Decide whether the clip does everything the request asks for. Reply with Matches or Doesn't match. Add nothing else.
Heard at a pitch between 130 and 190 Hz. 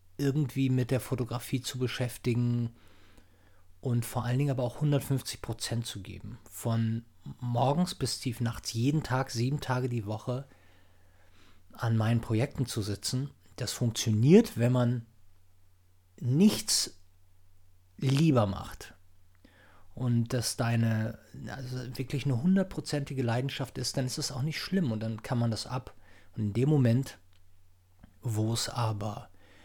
Doesn't match